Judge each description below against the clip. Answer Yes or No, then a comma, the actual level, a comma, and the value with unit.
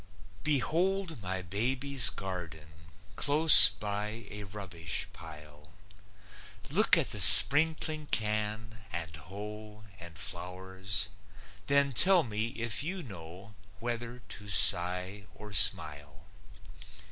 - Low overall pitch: Yes, low, 105 Hz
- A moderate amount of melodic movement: Yes, average, 4.9 semitones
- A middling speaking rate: No, slow, 100 wpm